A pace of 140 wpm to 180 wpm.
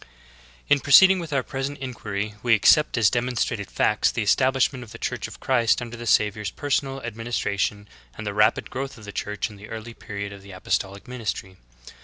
No: average, 195 wpm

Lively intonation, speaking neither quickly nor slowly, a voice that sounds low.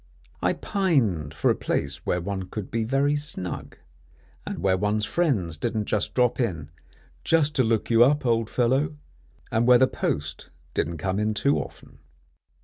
Yes: wide, 6.2 semitones; average, 160 wpm; low, 110 Hz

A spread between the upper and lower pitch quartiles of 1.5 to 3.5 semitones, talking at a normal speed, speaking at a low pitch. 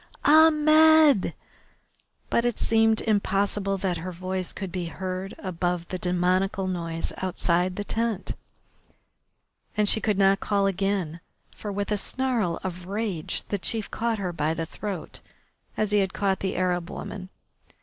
No: average, 2.7 semitones; average, 150 wpm; high, 195 Hz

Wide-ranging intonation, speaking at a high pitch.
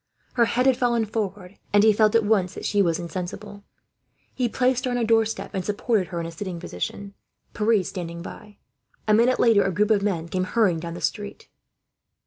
No: average, 3.6 semitones; high, 205 Hz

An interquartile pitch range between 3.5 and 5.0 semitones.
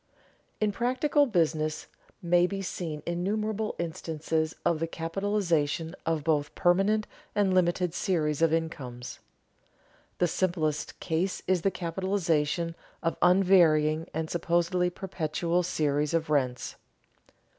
No: average, 3.0 semitones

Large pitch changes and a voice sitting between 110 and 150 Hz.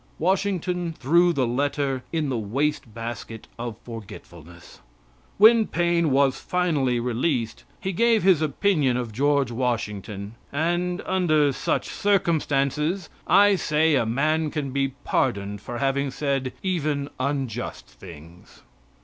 Yes: wide, 5.9 semitones; medium, 140 Hz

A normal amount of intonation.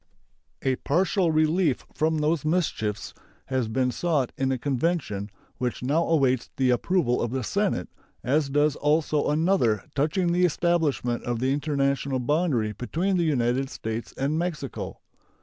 Yes: average, 4.6 semitones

